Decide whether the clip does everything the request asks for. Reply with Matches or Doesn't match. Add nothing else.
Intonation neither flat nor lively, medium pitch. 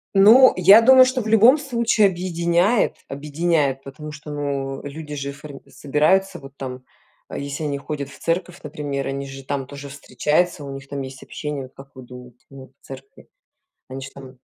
Matches